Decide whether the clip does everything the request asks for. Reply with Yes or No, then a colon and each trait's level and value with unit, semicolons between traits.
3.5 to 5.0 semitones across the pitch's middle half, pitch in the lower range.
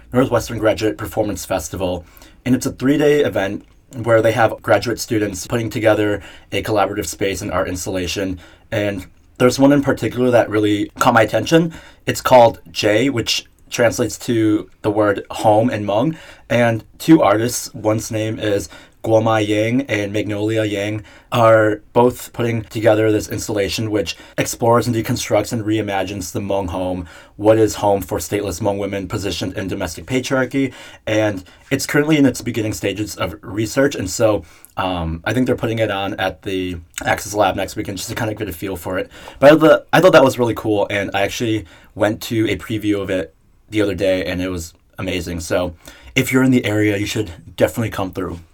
No: average, 3.1 semitones; low, 105 Hz